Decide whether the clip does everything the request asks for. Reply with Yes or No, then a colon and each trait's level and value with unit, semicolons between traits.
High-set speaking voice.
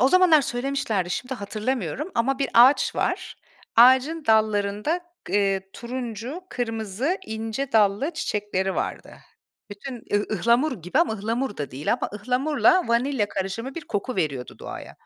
Yes: high, 230 Hz